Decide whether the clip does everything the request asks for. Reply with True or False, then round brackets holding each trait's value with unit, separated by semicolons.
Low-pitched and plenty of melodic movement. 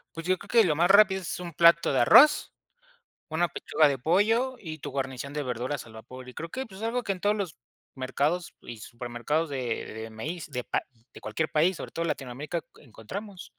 False (155 Hz; 6.4 semitones)